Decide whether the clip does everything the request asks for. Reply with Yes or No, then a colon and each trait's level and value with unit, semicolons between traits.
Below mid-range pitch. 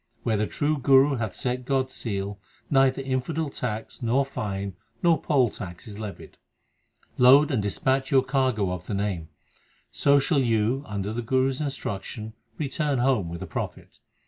Yes: low, 125 Hz